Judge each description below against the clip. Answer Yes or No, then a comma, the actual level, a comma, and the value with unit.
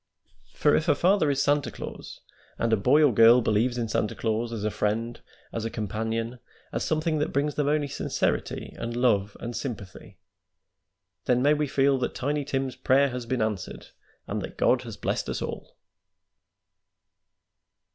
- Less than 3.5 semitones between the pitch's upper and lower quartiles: No, average, 4.1 semitones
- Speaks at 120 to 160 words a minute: No, average, 175 wpm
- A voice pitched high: No, low, 125 Hz